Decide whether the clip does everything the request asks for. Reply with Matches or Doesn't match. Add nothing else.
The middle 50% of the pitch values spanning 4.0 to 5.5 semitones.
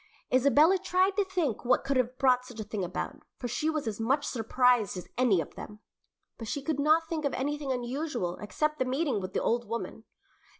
Matches